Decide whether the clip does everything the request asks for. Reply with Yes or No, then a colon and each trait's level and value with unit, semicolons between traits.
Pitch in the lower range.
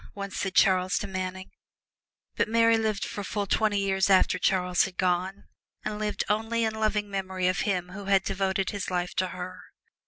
No: high, 195 Hz